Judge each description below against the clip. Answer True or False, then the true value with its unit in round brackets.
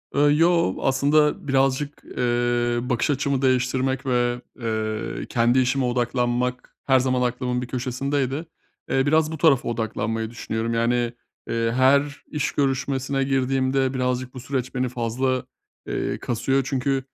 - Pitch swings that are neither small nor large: False (2.0 semitones)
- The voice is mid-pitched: False (130 Hz)